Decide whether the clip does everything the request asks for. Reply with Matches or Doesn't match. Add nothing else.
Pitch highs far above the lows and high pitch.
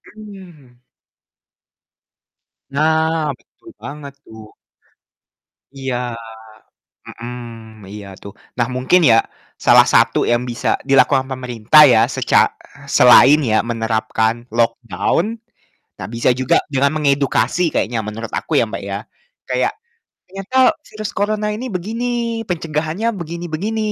Doesn't match